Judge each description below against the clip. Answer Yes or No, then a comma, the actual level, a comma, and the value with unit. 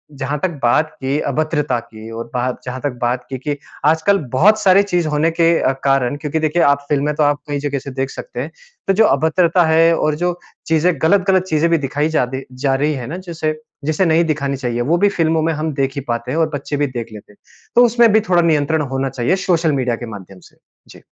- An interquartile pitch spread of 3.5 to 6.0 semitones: Yes, average, 3.8 semitones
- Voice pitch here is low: No, medium, 150 Hz